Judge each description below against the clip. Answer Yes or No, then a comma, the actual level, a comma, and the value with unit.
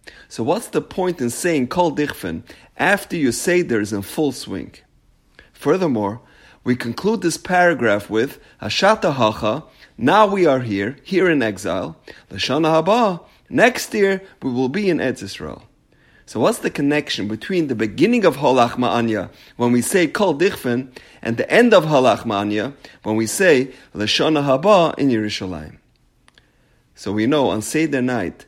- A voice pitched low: Yes, low, 130 Hz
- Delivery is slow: No, average, 150 wpm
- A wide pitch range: Yes, wide, 7.5 semitones